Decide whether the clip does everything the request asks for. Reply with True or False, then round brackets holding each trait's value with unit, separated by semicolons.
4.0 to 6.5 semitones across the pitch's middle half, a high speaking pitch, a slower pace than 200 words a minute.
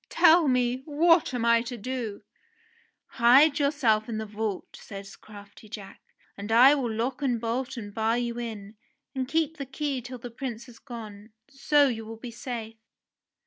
False (3.5 semitones; 240 Hz; 180 wpm)